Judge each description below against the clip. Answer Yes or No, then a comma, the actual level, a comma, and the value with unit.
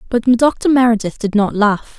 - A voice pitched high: Yes, high, 230 Hz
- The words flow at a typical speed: Yes, average, 180 wpm